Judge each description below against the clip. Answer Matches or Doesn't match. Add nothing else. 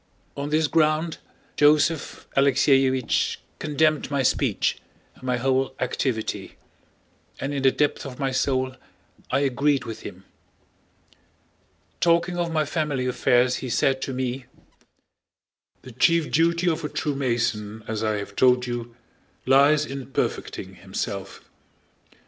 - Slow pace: Matches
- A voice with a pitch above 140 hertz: Doesn't match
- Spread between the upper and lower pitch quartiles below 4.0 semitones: Matches